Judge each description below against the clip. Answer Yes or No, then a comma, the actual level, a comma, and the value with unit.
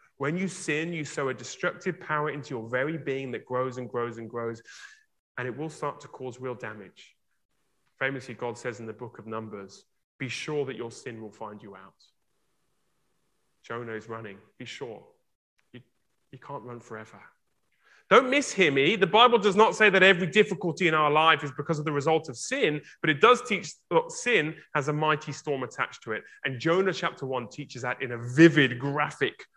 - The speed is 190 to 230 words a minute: Yes, average, 195 wpm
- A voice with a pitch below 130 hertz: No, medium, 140 Hz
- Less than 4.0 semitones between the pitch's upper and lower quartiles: No, average, 4.8 semitones